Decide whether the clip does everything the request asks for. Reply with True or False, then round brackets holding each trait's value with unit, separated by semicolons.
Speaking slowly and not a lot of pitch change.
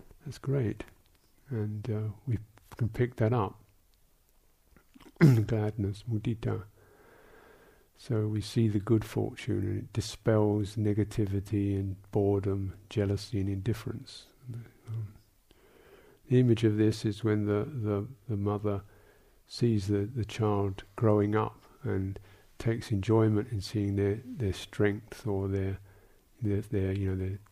True (125 wpm; 2.0 semitones)